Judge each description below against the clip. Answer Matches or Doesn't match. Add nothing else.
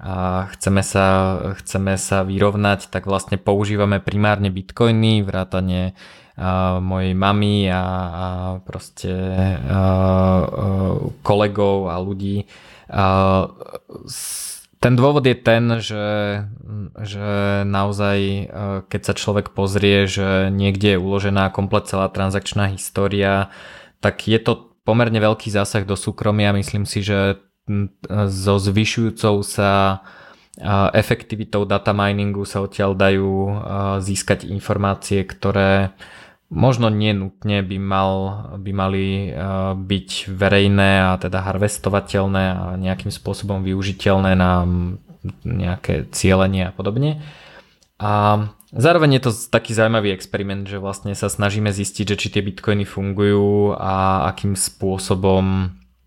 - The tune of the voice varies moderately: Doesn't match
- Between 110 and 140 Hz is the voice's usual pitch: Doesn't match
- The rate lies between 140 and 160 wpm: Doesn't match